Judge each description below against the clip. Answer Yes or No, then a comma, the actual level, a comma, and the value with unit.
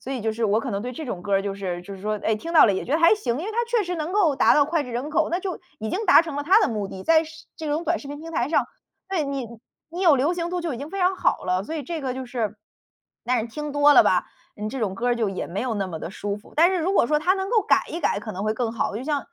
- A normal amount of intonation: No, wide, 7.4 semitones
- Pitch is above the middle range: Yes, very high, 275 Hz